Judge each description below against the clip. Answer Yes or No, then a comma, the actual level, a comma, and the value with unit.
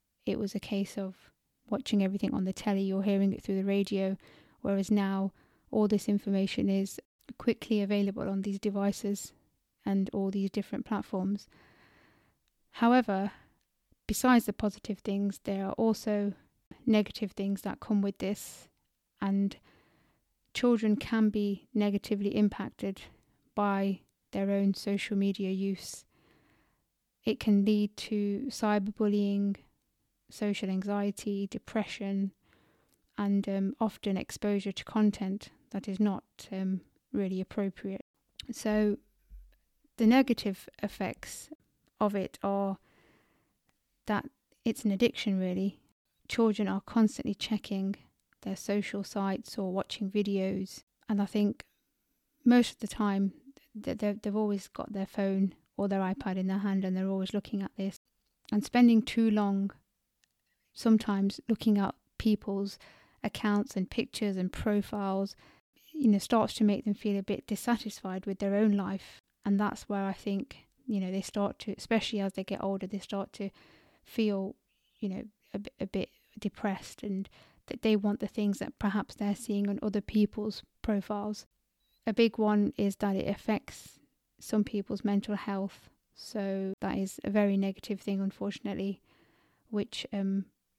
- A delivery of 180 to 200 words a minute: No, average, 140 wpm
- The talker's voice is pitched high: Yes, high, 205 Hz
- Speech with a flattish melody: Yes, narrow, 1.4 semitones